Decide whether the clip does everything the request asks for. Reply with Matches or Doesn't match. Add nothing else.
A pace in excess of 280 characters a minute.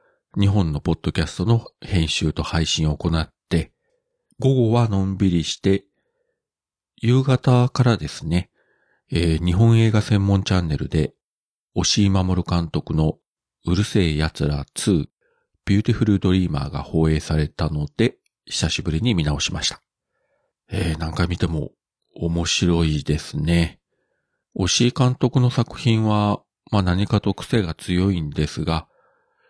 Doesn't match